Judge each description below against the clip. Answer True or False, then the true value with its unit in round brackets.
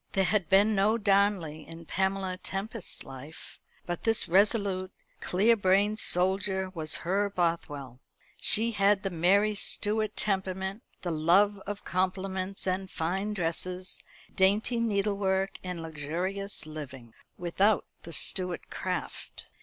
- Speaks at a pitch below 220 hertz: True (190 Hz)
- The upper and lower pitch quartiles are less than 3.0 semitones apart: True (2.6 semitones)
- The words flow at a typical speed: False (120 wpm)